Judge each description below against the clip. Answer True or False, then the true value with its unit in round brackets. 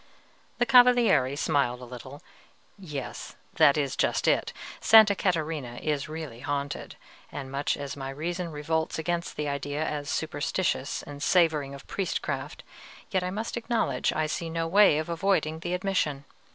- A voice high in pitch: False (155 Hz)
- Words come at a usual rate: True (150 wpm)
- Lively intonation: False (4.1 semitones)